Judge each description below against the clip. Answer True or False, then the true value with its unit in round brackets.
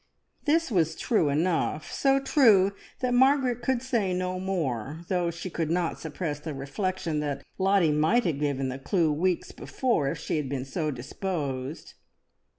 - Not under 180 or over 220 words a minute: False (160 wpm)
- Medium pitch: True (170 Hz)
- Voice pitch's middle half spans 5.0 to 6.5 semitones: True (5.3 semitones)